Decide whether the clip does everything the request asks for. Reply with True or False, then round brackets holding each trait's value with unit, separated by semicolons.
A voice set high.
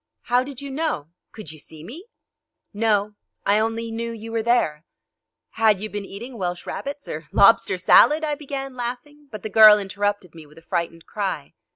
True (220 Hz)